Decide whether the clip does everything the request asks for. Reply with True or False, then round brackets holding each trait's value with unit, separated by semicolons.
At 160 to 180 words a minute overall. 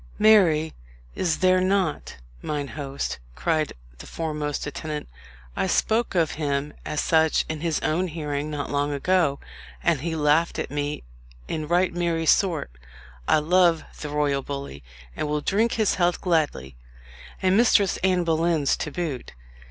False (150 wpm)